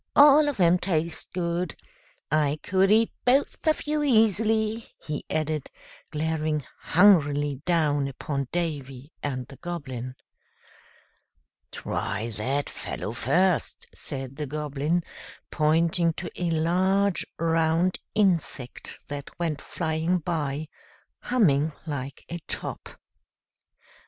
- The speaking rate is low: Yes, slow, 105 wpm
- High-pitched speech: No, medium, 160 Hz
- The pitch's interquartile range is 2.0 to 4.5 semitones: Yes, average, 4.0 semitones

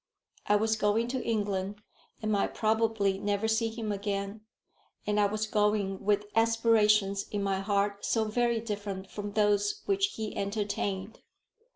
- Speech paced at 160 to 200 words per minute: No, average, 150 wpm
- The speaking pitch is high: Yes, high, 210 Hz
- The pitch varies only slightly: Yes, narrow, 1.7 semitones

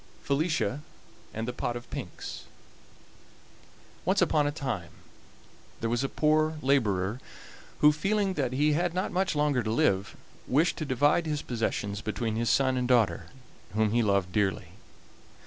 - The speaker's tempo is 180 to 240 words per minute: No, average, 150 wpm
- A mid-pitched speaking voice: No, low, 130 Hz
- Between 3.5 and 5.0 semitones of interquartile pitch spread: No, wide, 5.4 semitones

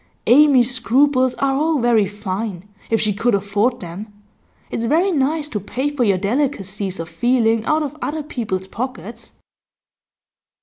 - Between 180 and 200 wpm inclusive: No, average, 145 wpm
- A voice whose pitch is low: No, high, 235 Hz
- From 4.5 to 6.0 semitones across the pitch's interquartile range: Yes, average, 5.1 semitones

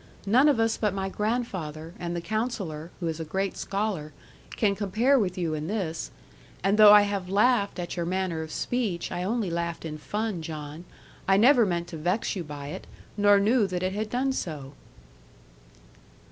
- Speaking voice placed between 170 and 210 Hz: Yes, high, 190 Hz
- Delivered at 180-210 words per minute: Yes, average, 190 wpm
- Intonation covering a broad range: No, average, 4.3 semitones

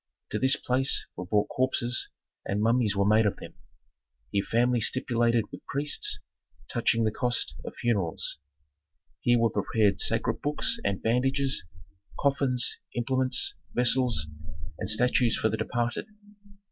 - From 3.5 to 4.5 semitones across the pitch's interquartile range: No, average, 2.8 semitones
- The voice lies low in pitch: Yes, low, 120 Hz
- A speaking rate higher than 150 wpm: No, slow, 135 wpm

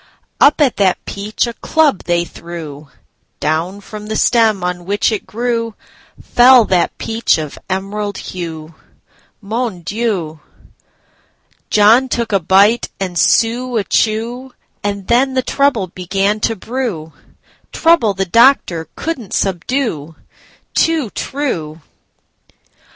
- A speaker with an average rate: No, slow, 105 wpm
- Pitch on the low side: No, high, 210 Hz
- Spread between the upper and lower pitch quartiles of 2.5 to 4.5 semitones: No, average, 5.1 semitones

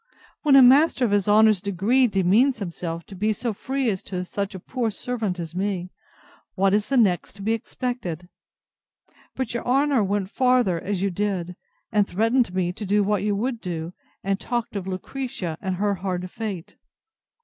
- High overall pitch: Yes, high, 205 Hz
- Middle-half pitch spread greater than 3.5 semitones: Yes, average, 4.5 semitones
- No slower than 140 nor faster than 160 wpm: No, average, 175 wpm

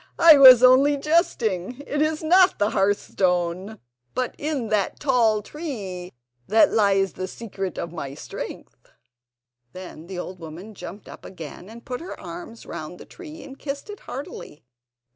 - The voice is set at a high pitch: Yes, high, 220 Hz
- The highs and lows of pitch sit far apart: Yes, wide, 7.3 semitones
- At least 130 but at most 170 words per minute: Yes, average, 160 wpm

